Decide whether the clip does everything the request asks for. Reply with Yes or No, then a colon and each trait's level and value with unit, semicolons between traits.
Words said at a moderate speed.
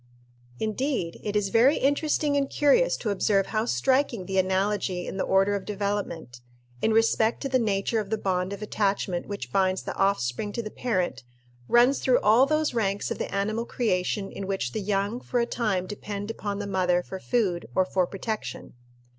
Yes: average, 190 wpm